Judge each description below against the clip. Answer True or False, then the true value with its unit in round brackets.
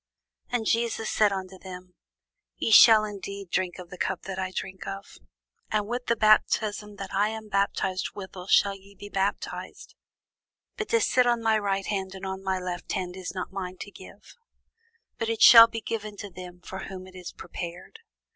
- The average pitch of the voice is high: True (195 Hz)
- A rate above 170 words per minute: True (190 wpm)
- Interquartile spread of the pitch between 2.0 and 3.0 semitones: True (2.4 semitones)